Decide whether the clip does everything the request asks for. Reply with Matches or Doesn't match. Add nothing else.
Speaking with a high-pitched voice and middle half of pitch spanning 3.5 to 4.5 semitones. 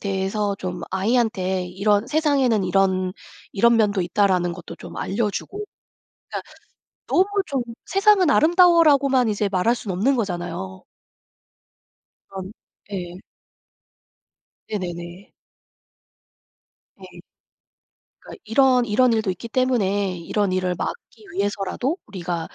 Doesn't match